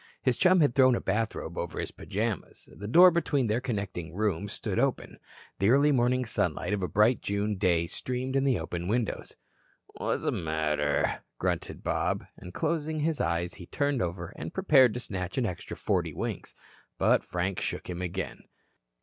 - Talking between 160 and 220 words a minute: Yes, average, 170 wpm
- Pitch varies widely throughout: Yes, wide, 6.6 semitones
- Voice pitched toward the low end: Yes, low, 105 Hz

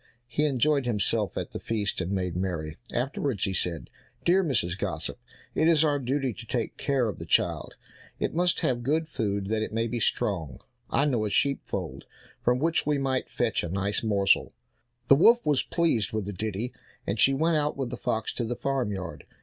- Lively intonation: Yes, wide, 5.9 semitones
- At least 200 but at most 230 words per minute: Yes, fast, 205 wpm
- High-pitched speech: No, low, 120 Hz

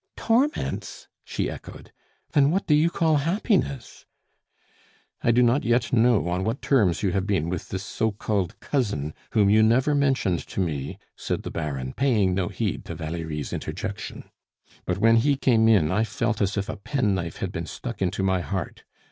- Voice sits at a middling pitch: No, low, 105 Hz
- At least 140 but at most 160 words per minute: No, average, 180 wpm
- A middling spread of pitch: No, wide, 5.9 semitones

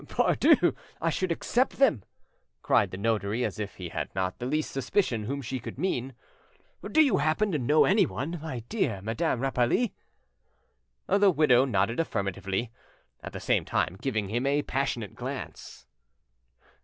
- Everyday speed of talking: Yes, average, 155 wpm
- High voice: No, low, 130 Hz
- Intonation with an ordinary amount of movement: No, wide, 6.4 semitones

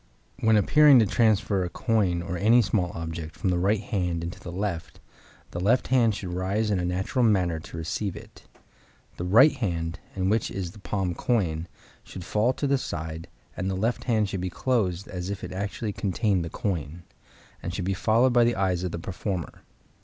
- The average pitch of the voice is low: Yes, very low, 95 Hz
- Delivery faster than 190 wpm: Yes, average, 200 wpm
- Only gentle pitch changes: No, average, 3.8 semitones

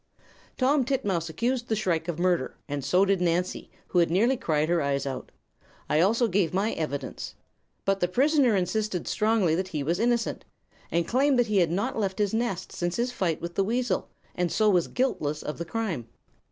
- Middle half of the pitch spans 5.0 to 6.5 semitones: Yes, average, 5.3 semitones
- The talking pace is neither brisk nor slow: Yes, average, 195 wpm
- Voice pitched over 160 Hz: Yes, high, 190 Hz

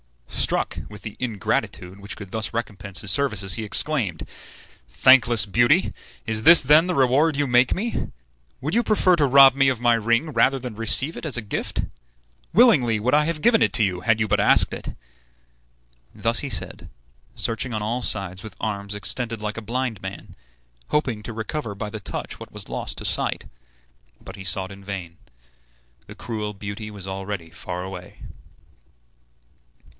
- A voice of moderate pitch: No, low, 110 Hz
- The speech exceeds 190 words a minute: No, average, 175 wpm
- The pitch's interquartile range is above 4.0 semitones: Yes, average, 4.8 semitones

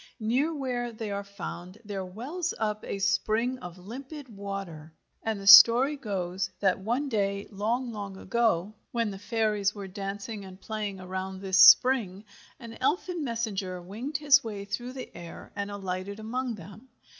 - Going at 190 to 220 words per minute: No, average, 160 wpm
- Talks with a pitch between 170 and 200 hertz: No, high, 210 Hz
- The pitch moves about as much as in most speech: Yes, average, 3.7 semitones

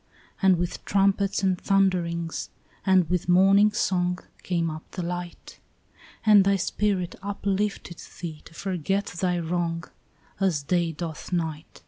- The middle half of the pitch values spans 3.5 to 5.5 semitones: No, narrow, 2.4 semitones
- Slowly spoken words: Yes, slow, 130 wpm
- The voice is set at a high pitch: No, medium, 180 Hz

